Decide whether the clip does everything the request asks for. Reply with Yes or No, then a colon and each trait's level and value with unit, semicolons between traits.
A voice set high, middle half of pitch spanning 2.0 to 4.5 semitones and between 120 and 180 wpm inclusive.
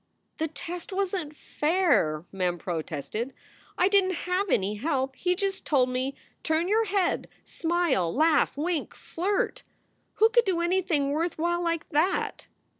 No: very high, 330 Hz; wide, 5.5 semitones; average, 150 wpm